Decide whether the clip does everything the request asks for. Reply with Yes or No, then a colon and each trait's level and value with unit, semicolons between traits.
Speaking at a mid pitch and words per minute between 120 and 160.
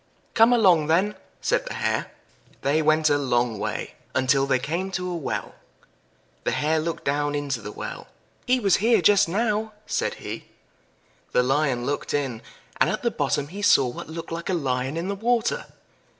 No: medium, 160 Hz; average, 180 wpm